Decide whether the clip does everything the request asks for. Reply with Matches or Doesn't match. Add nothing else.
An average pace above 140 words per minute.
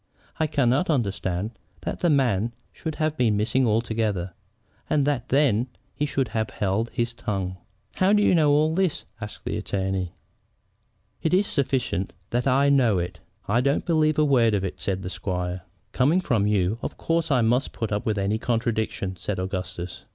Matches